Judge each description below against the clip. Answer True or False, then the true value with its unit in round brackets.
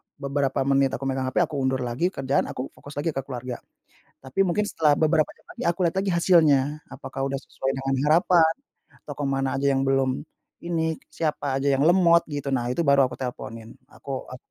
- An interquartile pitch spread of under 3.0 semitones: False (3.3 semitones)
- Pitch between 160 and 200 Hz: False (140 Hz)